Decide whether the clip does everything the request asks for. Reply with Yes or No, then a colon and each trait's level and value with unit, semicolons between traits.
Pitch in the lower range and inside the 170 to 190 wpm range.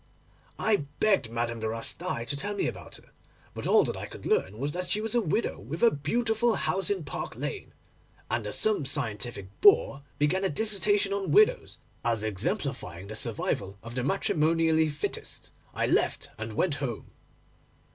No: medium, 150 Hz; average, 175 wpm